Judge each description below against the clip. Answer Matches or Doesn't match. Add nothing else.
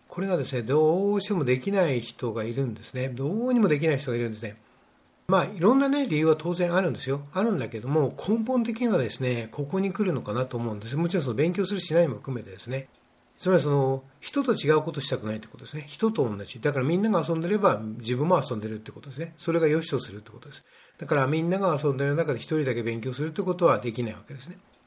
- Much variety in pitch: Matches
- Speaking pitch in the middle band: Matches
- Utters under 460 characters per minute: Doesn't match